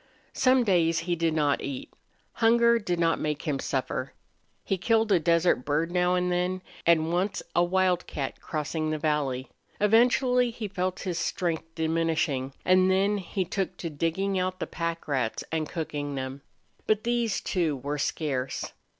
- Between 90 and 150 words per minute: No, average, 160 wpm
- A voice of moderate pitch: Yes, medium, 170 Hz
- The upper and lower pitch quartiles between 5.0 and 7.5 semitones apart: No, average, 3.7 semitones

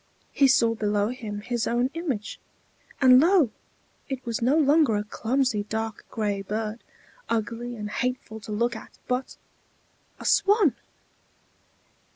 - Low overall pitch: No, high, 235 Hz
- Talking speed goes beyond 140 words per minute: No, slow, 135 wpm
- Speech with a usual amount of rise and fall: Yes, average, 3.5 semitones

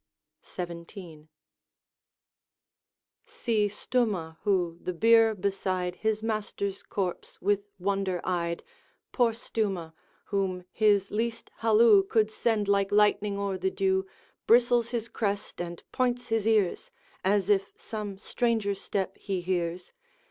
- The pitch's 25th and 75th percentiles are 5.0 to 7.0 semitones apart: No, average, 2.9 semitones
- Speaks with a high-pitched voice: Yes, high, 200 Hz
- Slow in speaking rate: Yes, slow, 120 wpm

